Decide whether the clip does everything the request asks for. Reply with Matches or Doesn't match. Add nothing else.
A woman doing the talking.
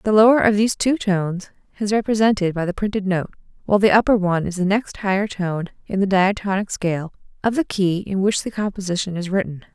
Matches